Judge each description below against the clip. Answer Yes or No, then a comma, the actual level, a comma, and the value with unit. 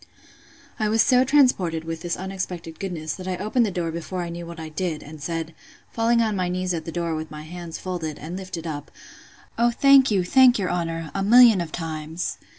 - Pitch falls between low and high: Yes, medium, 175 Hz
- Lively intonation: No, average, 3.4 semitones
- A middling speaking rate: No, fast, 215 wpm